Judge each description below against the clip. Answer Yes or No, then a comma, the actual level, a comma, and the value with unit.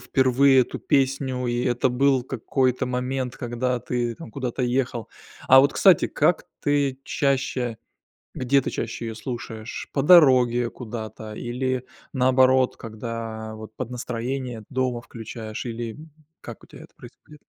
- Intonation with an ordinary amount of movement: No, narrow, 2.0 semitones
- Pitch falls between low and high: No, low, 125 Hz